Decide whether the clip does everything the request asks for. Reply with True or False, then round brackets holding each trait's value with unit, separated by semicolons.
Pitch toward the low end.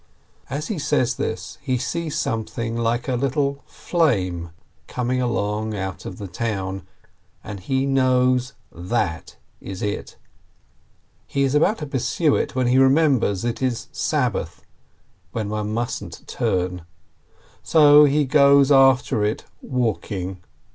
True (120 Hz)